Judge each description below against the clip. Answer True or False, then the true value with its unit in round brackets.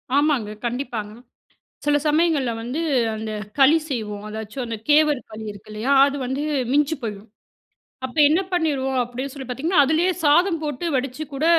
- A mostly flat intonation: False (4.5 semitones)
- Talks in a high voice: True (270 Hz)